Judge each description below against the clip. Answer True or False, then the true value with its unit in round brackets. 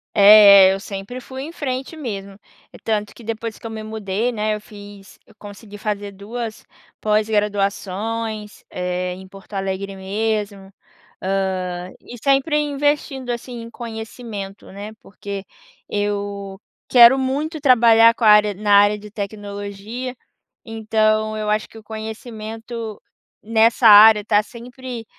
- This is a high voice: True (215 Hz)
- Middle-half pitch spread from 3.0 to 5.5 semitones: False (2.4 semitones)